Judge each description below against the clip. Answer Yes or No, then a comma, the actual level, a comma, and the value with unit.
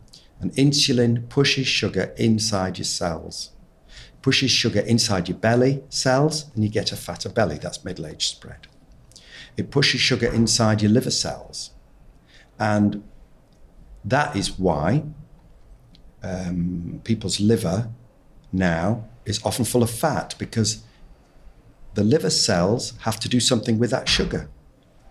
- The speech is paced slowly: Yes, slow, 130 wpm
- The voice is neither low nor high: No, low, 115 Hz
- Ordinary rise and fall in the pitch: Yes, average, 3.9 semitones